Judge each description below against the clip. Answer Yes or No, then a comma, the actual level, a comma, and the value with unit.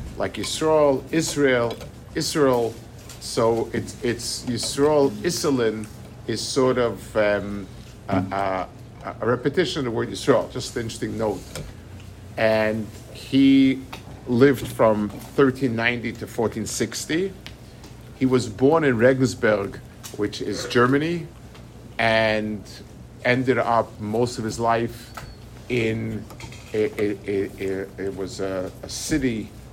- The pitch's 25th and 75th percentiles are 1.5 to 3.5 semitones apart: Yes, average, 2.9 semitones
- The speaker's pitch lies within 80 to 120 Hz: Yes, low, 115 Hz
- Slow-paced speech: Yes, slow, 115 wpm